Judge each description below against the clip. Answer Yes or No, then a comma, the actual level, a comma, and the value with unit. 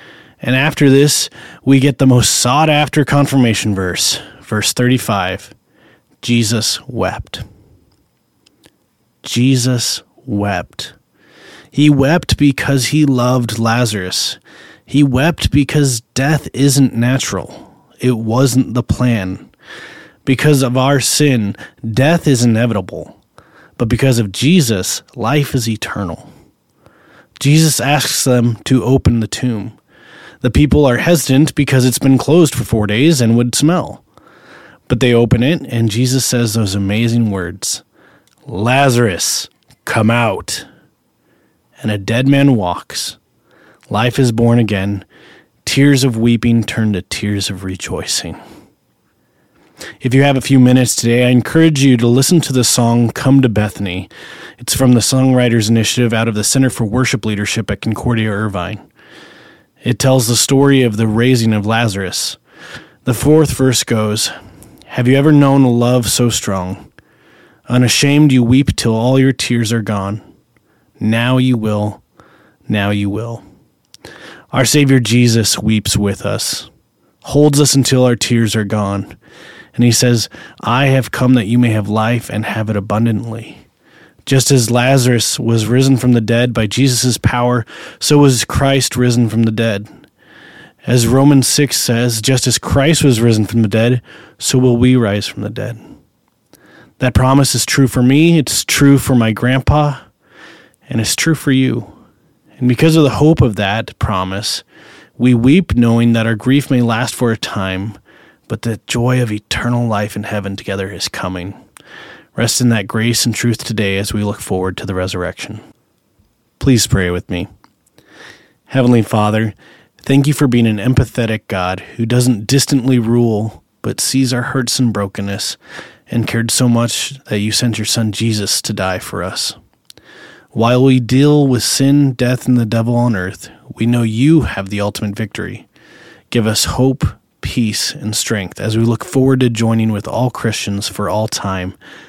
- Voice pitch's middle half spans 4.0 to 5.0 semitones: No, average, 3.5 semitones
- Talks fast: No, average, 155 wpm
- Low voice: Yes, low, 120 Hz